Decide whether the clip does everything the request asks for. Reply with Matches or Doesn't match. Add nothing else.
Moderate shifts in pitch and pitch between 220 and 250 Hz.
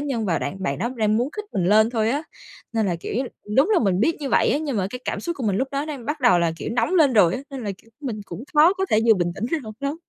Doesn't match